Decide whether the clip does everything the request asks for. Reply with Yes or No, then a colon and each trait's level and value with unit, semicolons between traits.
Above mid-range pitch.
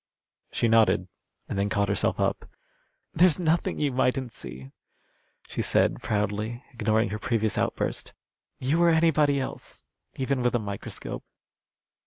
No: low, 120 Hz